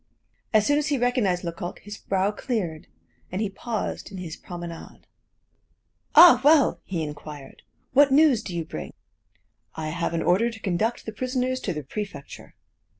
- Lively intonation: Yes, wide, 6.5 semitones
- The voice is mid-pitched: No, high, 200 Hz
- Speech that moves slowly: No, average, 160 wpm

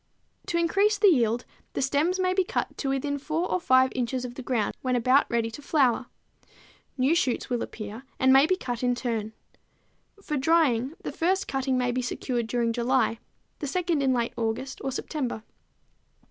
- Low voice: No, very high, 260 Hz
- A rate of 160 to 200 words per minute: Yes, average, 185 wpm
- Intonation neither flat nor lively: Yes, average, 4.2 semitones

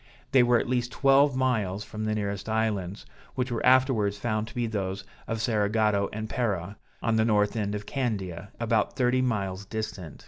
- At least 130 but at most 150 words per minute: No, average, 180 wpm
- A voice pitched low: Yes, low, 110 Hz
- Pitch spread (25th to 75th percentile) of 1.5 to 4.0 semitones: Yes, average, 3.1 semitones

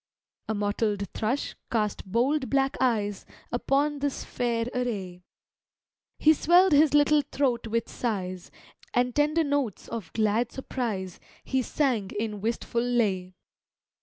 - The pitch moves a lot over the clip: No, average, 4.8 semitones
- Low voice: No, high, 235 Hz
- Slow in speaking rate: Yes, slow, 125 wpm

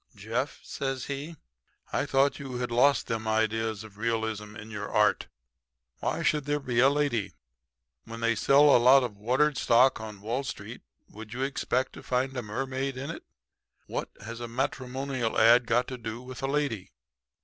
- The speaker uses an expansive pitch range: No, average, 3.2 semitones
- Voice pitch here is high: No, low, 125 Hz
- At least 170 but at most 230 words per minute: Yes, average, 180 wpm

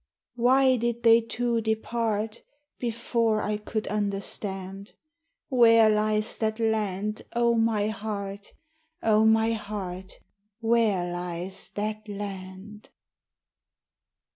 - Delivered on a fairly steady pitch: Yes, narrow, 2.2 semitones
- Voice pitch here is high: Yes, high, 215 Hz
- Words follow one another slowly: Yes, slow, 95 wpm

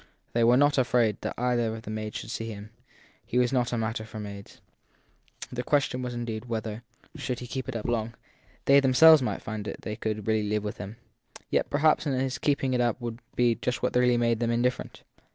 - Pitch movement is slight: Yes, narrow, 2.3 semitones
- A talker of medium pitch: No, low, 120 Hz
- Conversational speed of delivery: No, fast, 220 wpm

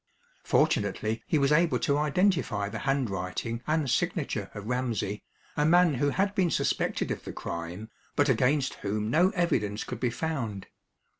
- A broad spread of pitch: Yes, wide, 6.8 semitones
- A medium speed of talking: Yes, average, 155 wpm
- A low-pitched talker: Yes, low, 130 Hz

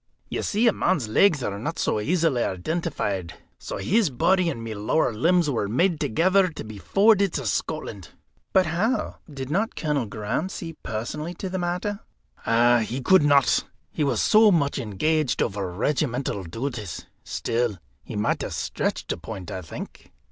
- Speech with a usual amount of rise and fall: No, wide, 8.4 semitones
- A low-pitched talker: No, medium, 145 Hz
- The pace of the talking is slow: No, average, 170 wpm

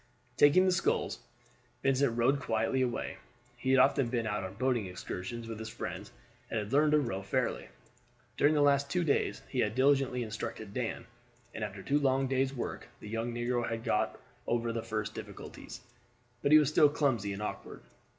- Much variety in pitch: No, average, 4.0 semitones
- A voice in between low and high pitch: No, low, 120 Hz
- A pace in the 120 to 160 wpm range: No, average, 185 wpm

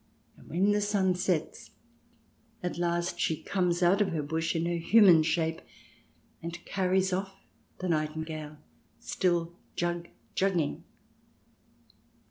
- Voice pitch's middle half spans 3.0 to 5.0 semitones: No, narrow, 2.4 semitones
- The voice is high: No, medium, 175 Hz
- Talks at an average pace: No, slow, 120 wpm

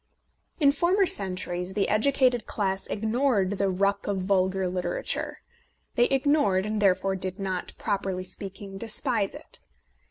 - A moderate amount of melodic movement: Yes, average, 4.1 semitones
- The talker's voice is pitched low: No, high, 200 Hz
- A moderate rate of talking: No, slow, 130 wpm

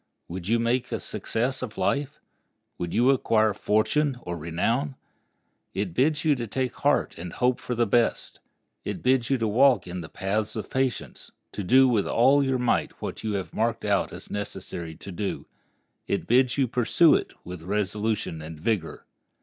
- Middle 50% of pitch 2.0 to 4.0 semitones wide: No, average, 5.1 semitones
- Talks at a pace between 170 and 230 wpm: Yes, average, 175 wpm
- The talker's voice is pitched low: Yes, low, 115 Hz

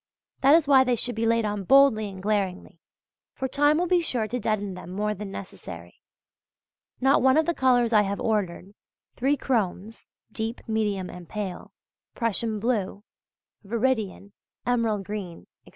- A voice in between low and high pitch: No, high, 220 Hz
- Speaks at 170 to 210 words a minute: No, average, 160 wpm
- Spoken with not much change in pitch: No, average, 4.1 semitones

